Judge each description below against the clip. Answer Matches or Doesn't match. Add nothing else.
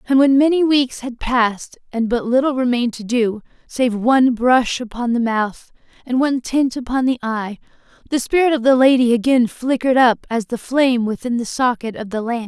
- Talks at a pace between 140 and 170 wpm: Doesn't match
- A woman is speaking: Matches